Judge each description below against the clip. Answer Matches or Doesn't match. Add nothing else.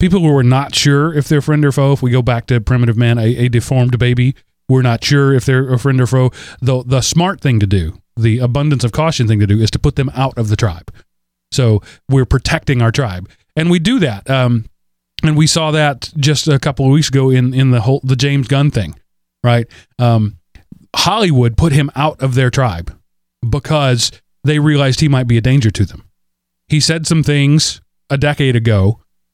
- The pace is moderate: Doesn't match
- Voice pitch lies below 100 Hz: Doesn't match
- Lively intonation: Doesn't match